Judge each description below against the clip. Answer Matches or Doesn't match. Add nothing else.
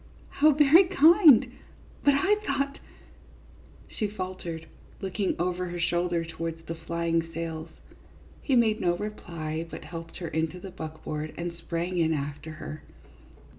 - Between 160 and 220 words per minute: Doesn't match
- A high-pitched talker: Doesn't match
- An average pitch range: Matches